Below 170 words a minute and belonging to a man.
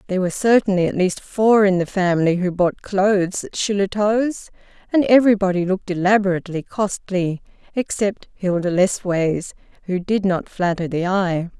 No: average, 145 wpm; female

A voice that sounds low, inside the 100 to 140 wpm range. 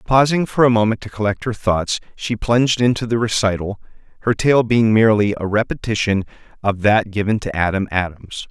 No: low, 110 Hz; average, 175 wpm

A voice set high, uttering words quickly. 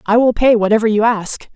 Yes: high, 220 Hz; fast, 230 wpm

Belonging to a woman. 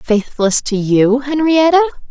Yes: female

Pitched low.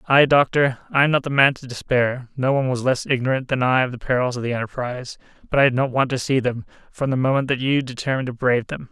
Yes: low, 130 Hz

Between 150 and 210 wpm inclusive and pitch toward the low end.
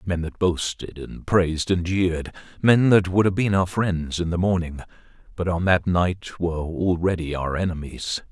Yes: average, 175 wpm; very low, 90 Hz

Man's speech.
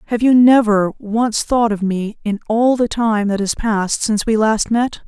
No: female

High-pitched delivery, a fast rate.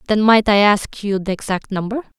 Yes: high, 205 Hz; fast, 220 wpm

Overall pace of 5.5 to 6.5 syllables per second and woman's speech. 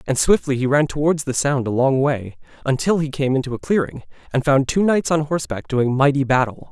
No: 5.7 syllables/s; male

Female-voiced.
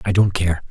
No: male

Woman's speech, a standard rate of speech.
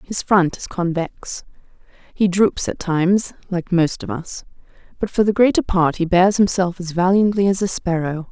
Yes: female; average, 180 wpm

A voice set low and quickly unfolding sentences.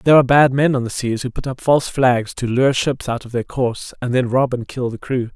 Yes: low, 125 Hz; fast, 290 wpm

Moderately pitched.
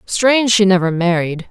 No: high, 195 Hz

